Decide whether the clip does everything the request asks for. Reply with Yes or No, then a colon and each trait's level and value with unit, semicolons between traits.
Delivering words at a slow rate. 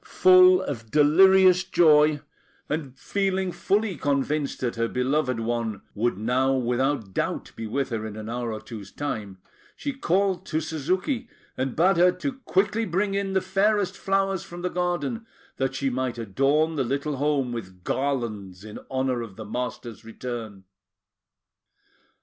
No: average, 155 wpm